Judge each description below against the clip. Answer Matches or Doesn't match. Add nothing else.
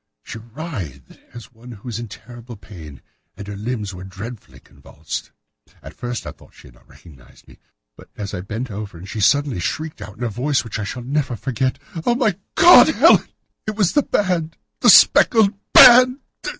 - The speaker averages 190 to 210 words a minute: Matches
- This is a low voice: Matches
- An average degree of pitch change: Doesn't match